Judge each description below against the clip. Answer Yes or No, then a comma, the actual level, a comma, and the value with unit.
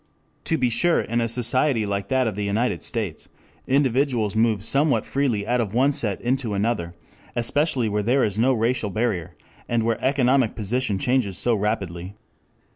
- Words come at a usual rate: Yes, average, 170 wpm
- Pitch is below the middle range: Yes, low, 115 Hz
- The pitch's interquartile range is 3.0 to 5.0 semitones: Yes, average, 3.8 semitones